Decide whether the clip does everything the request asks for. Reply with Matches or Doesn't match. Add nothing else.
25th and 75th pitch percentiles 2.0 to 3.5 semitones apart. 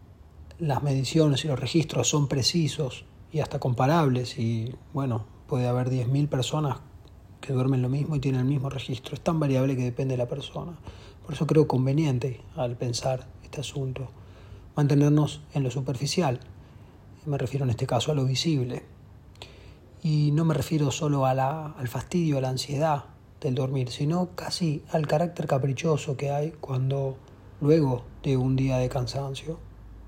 Matches